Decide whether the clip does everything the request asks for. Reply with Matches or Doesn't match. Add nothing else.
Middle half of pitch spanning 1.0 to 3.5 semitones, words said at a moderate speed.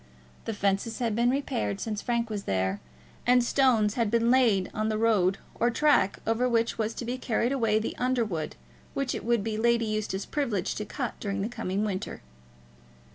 Matches